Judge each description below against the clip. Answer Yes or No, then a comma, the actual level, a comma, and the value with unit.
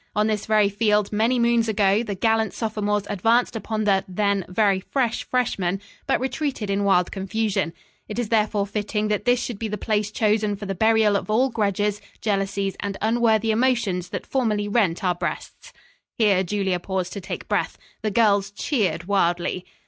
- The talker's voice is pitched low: No, high, 210 Hz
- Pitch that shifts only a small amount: Yes, narrow, 2.2 semitones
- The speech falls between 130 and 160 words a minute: No, average, 175 wpm